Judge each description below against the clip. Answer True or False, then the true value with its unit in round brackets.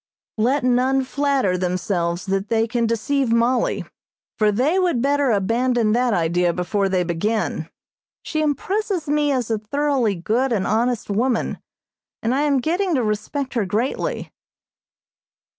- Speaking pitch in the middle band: False (235 Hz)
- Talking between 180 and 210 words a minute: False (140 wpm)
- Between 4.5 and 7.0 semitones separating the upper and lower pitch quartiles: True (5.2 semitones)